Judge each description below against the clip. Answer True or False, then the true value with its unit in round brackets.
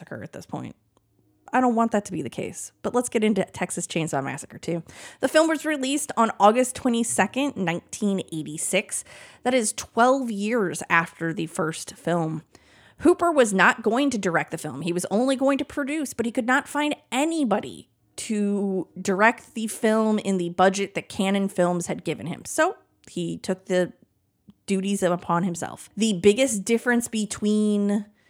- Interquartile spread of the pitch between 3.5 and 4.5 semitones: False (5.6 semitones)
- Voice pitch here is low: False (205 Hz)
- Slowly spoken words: False (170 wpm)